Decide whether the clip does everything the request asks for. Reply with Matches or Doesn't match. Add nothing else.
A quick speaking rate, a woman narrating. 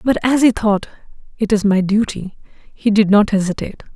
Doesn't match